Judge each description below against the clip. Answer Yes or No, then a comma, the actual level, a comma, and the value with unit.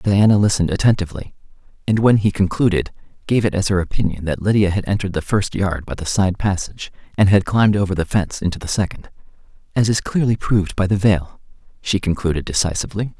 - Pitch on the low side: Yes, very low, 95 Hz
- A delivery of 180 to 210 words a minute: Yes, average, 190 wpm